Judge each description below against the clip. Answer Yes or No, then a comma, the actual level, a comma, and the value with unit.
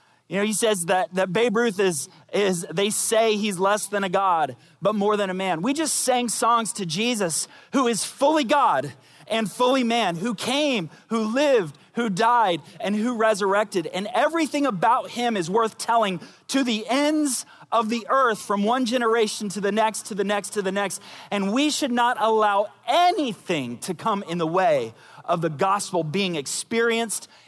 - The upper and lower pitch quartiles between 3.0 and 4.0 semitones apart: Yes, average, 3.6 semitones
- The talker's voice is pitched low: No, high, 215 Hz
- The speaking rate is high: No, average, 185 wpm